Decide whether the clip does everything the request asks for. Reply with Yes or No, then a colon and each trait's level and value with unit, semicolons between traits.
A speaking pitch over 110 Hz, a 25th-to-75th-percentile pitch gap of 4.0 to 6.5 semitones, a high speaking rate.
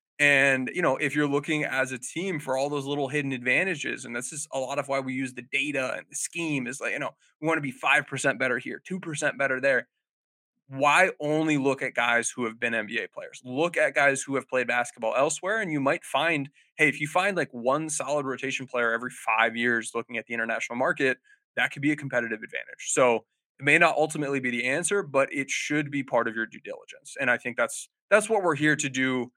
No: low, 135 Hz; average, 3.2 semitones; fast, 235 wpm